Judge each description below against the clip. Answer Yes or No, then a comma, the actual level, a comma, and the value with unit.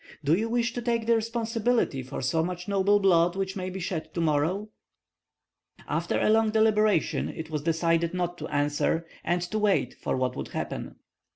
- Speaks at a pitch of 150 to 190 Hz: Yes, medium, 185 Hz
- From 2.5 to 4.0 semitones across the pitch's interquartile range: No, average, 4.9 semitones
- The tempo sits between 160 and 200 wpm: Yes, average, 185 wpm